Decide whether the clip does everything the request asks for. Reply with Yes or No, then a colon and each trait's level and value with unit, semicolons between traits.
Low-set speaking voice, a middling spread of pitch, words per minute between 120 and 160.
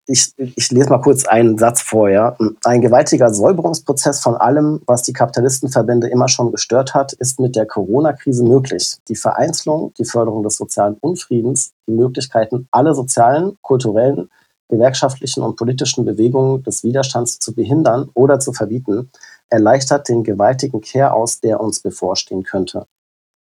Yes: low, 125 Hz; average, 3.0 semitones; average, 145 wpm